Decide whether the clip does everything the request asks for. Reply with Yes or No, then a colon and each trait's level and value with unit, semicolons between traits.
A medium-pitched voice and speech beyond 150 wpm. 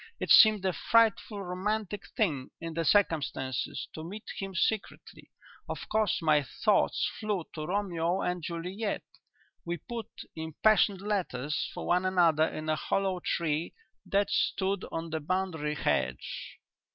No: medium, 180 Hz; average, 140 wpm